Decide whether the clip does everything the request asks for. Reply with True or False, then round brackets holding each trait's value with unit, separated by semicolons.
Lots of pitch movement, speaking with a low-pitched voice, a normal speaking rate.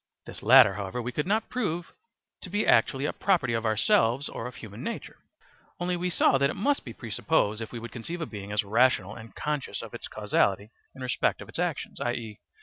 False (6.6 semitones; 125 Hz; 215 wpm)